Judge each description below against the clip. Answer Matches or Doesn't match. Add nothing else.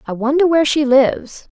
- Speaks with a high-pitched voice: Matches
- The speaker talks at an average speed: Matches